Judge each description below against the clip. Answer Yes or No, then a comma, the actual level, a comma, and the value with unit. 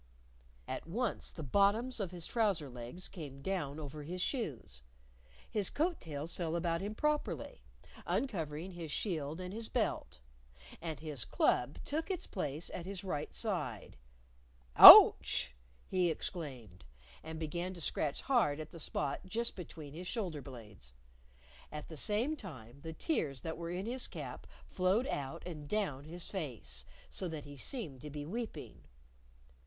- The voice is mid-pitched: Yes, medium, 165 Hz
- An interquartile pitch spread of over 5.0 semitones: Yes, wide, 5.4 semitones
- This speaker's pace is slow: No, average, 155 wpm